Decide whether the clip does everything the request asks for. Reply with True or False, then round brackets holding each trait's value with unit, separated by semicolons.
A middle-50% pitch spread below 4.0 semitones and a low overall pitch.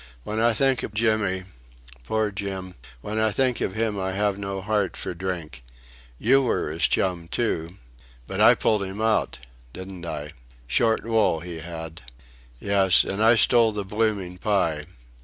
True (3.6 semitones; 100 Hz)